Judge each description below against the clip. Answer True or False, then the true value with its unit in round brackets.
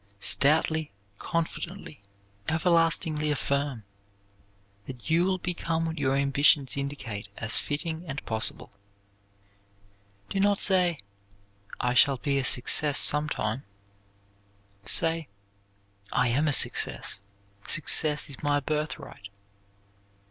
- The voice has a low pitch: False (150 Hz)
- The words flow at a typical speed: False (100 wpm)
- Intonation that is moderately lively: True (3.3 semitones)